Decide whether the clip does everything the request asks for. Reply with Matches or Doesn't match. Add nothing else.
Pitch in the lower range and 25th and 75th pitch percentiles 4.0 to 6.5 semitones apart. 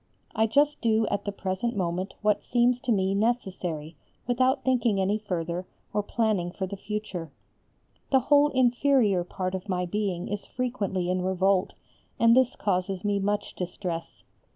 Doesn't match